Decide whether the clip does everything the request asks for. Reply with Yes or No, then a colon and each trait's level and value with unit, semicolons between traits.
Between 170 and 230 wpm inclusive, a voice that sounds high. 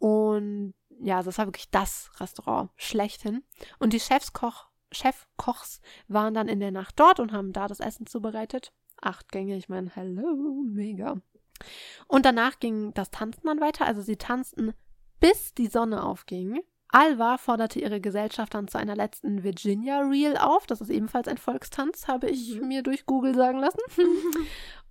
No: average, 160 wpm; high, 230 Hz